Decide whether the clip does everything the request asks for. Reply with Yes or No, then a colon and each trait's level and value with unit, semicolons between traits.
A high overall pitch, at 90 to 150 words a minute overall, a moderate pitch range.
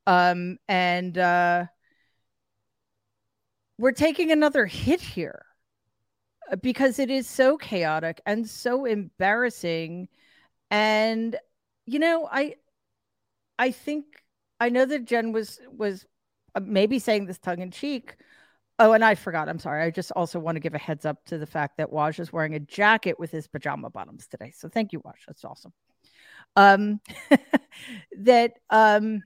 No: high, 195 Hz; average, 145 wpm; wide, 6.7 semitones